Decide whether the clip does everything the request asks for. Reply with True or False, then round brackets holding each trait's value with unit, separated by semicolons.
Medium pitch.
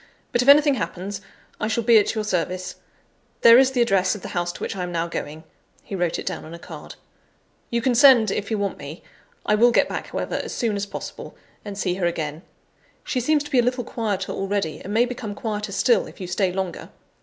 False (205 Hz)